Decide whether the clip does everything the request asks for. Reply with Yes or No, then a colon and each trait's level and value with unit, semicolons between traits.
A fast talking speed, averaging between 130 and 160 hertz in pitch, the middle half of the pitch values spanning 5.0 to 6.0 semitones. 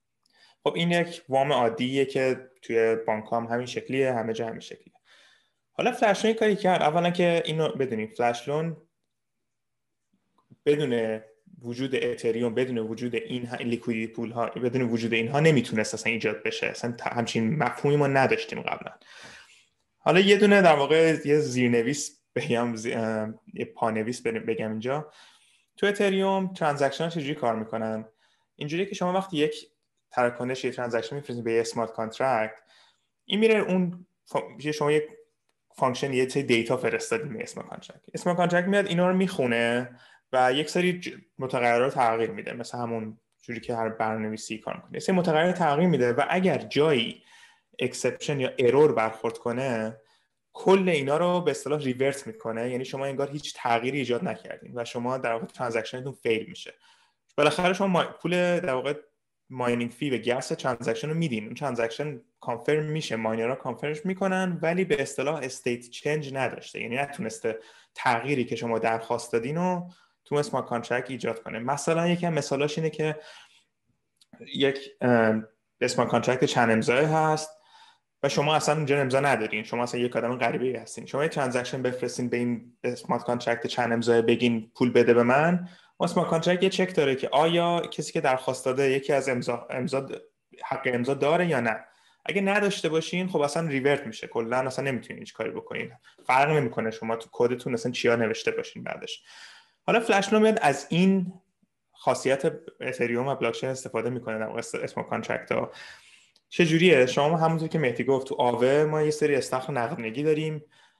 Yes: fast, 160 wpm; low, 135 Hz; wide, 5.5 semitones